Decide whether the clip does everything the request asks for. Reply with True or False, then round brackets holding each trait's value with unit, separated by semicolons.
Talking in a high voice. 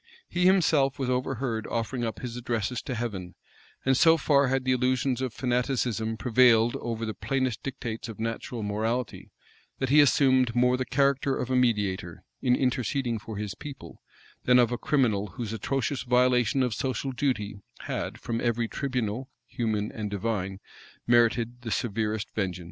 False (120 Hz)